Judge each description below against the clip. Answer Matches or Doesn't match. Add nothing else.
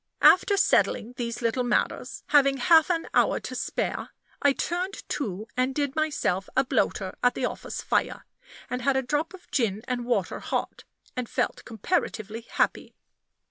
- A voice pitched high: Matches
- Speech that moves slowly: Doesn't match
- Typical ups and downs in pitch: Matches